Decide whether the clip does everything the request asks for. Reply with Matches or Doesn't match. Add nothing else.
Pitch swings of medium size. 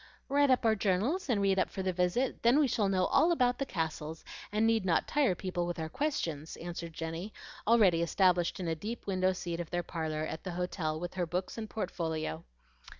Matches